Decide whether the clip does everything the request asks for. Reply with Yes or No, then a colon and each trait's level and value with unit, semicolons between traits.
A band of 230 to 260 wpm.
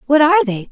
Yes: fast, 250 wpm